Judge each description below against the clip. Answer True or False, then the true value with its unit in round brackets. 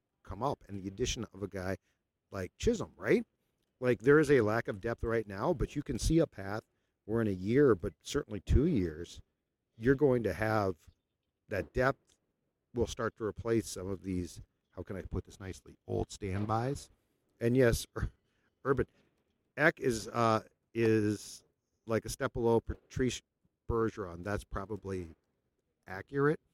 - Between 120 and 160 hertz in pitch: False (105 Hz)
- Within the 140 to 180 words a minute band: True (160 wpm)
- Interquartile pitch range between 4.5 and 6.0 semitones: False (3.7 semitones)